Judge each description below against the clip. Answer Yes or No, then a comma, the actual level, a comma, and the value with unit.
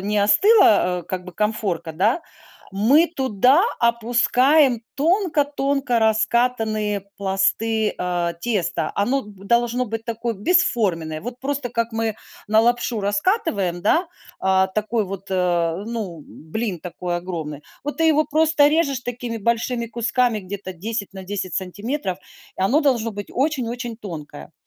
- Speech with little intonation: No, average, 4.7 semitones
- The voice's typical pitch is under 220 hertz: No, high, 225 Hz